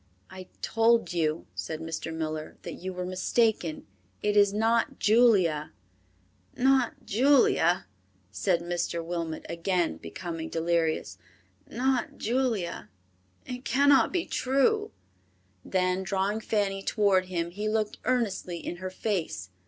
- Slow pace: Yes, slow, 120 wpm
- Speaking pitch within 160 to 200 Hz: Yes, medium, 185 Hz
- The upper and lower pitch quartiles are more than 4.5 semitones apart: Yes, average, 5.0 semitones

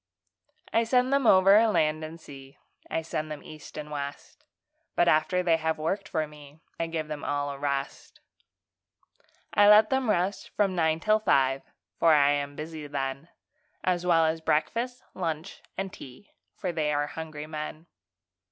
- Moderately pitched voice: Yes, medium, 160 Hz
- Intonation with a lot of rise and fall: No, average, 3.9 semitones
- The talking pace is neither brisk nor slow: Yes, average, 165 wpm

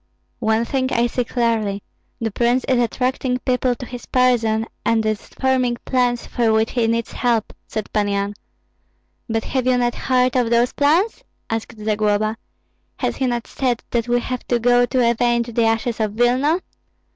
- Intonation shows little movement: Yes, narrow, 2.0 semitones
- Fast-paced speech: No, average, 175 wpm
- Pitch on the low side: No, high, 240 Hz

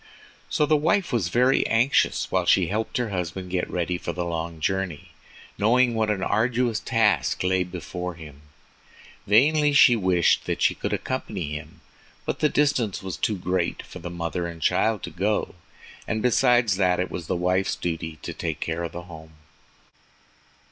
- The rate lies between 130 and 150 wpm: No, average, 175 wpm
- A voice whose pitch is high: No, very low, 95 Hz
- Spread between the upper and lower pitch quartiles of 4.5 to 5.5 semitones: Yes, average, 5.2 semitones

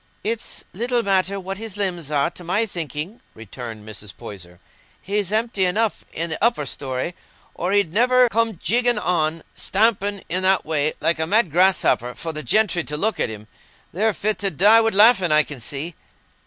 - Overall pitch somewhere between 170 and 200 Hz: Yes, medium, 185 Hz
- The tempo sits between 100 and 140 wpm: No, average, 185 wpm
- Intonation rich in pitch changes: Yes, wide, 5.9 semitones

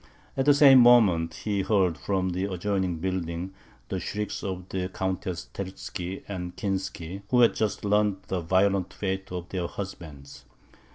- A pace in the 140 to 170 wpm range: Yes, average, 155 wpm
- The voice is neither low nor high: No, very low, 95 Hz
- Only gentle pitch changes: Yes, narrow, 2.2 semitones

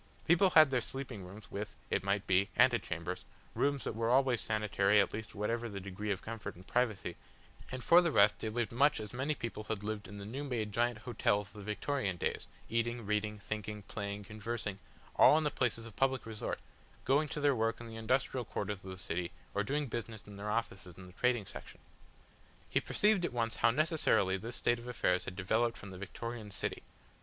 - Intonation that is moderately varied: Yes, average, 3.4 semitones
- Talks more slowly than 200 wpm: No, fast, 205 wpm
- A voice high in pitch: No, low, 110 Hz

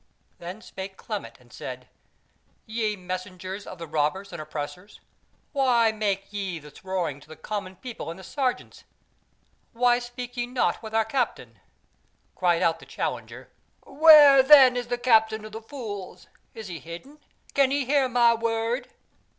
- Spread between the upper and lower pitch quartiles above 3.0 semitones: Yes, average, 5.0 semitones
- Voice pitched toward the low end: No, high, 220 Hz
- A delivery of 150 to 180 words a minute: Yes, average, 160 wpm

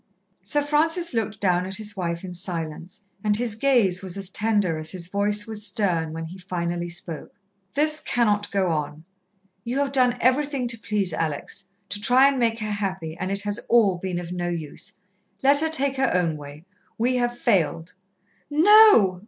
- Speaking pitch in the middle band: No, high, 205 Hz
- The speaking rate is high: No, average, 185 wpm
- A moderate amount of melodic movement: No, wide, 5.8 semitones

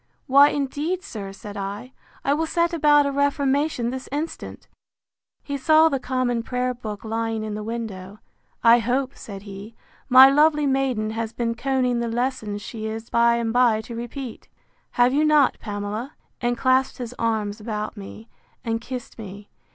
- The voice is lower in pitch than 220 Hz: No, high, 240 Hz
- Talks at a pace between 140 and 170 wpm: Yes, average, 165 wpm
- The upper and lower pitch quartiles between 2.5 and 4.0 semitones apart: Yes, average, 3.7 semitones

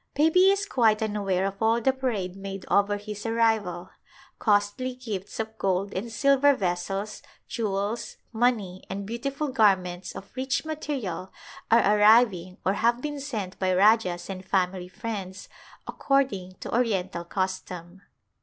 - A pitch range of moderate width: Yes, average, 4.1 semitones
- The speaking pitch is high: Yes, high, 205 Hz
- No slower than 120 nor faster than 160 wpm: Yes, average, 140 wpm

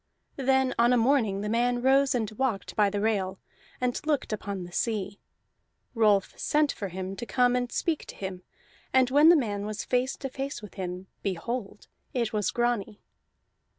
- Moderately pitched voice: No, high, 230 Hz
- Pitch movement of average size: Yes, average, 4.2 semitones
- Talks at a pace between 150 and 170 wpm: No, average, 180 wpm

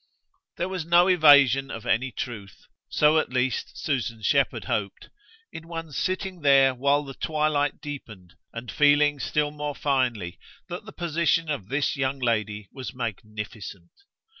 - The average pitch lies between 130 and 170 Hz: Yes, medium, 140 Hz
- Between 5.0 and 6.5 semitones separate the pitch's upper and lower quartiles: No, average, 4.6 semitones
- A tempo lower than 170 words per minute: Yes, average, 145 wpm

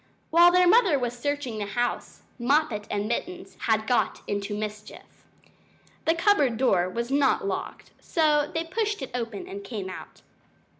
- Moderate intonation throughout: No, wide, 7.2 semitones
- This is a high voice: Yes, high, 245 Hz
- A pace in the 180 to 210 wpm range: No, average, 155 wpm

